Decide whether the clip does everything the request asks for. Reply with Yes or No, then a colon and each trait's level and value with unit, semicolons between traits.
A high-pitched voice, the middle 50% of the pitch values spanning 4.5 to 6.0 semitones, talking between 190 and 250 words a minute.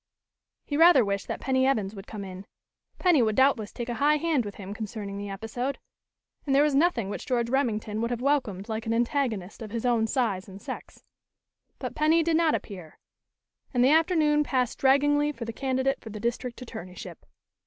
Yes: high, 240 Hz; average, 5.0 semitones; average, 195 wpm